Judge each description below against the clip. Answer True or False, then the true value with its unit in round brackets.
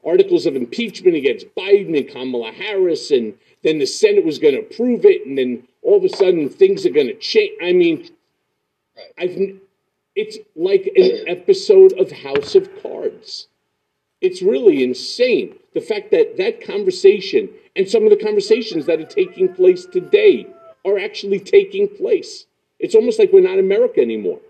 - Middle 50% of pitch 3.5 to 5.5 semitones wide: False (2.5 semitones)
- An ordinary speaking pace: True (170 wpm)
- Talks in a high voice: True (395 Hz)